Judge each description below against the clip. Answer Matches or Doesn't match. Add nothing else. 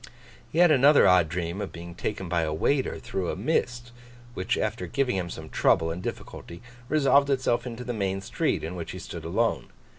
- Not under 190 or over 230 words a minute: Matches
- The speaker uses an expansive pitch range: Matches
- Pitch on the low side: Matches